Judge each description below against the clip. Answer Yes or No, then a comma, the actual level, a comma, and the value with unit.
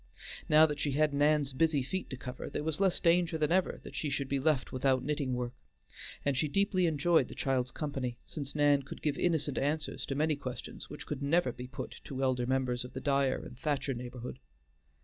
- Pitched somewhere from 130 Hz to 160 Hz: Yes, medium, 140 Hz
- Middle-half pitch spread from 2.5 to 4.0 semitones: Yes, average, 2.9 semitones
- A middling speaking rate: No, fast, 210 wpm